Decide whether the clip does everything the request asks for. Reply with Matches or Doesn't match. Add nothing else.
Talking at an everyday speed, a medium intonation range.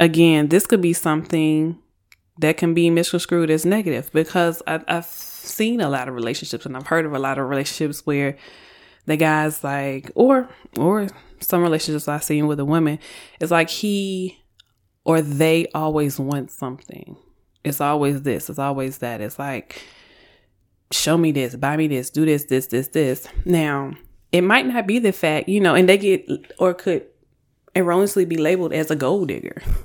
Matches